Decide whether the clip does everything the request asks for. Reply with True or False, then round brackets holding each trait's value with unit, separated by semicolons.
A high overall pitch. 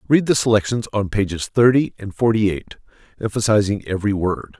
False (105 Hz)